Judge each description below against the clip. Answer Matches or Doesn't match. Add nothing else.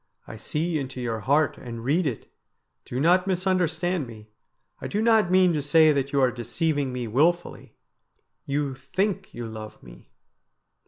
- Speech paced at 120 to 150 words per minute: Doesn't match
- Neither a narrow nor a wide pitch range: Doesn't match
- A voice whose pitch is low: Doesn't match